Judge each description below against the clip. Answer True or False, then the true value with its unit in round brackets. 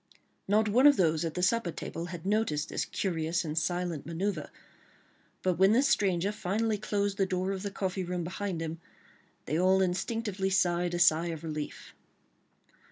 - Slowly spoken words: False (170 wpm)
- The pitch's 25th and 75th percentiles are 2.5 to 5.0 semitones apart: True (3.1 semitones)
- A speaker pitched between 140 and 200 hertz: True (185 Hz)